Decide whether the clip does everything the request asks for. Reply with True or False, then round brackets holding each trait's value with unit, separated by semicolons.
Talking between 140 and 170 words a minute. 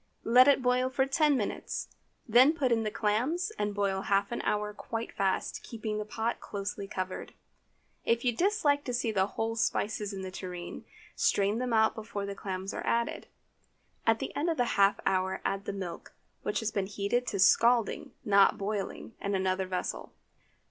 False (185 wpm)